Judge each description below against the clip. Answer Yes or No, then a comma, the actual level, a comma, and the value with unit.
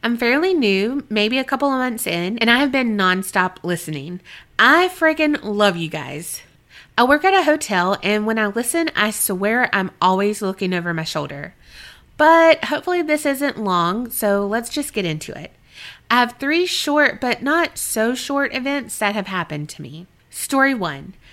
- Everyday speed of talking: Yes, average, 180 wpm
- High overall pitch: Yes, high, 225 Hz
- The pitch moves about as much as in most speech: No, wide, 7.1 semitones